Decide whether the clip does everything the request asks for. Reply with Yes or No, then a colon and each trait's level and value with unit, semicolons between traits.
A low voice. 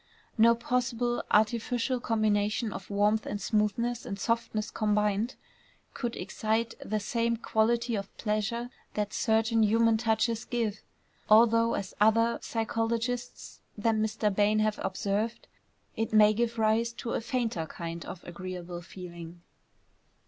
No: high, 220 Hz